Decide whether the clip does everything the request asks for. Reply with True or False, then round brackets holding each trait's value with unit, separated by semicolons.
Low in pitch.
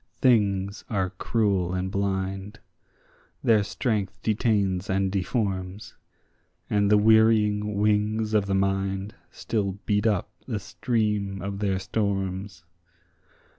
True (100 Hz)